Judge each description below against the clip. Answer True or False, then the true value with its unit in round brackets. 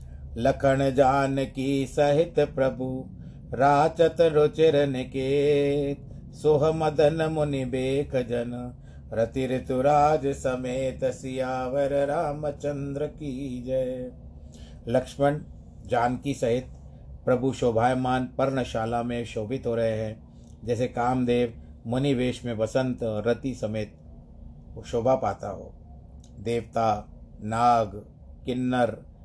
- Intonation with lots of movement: False (2.9 semitones)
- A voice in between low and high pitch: False (130 Hz)